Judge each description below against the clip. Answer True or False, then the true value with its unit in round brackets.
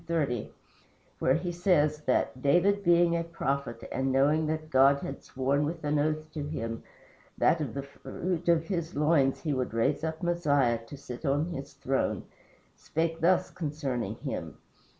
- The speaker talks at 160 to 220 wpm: True (165 wpm)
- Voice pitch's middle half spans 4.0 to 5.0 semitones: False (3.5 semitones)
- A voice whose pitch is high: False (150 Hz)